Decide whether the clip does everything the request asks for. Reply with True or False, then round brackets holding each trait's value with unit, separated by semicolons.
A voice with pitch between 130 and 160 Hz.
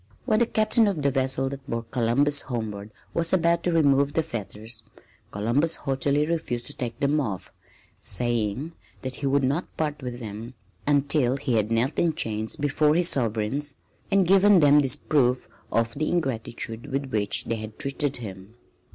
True (135 Hz)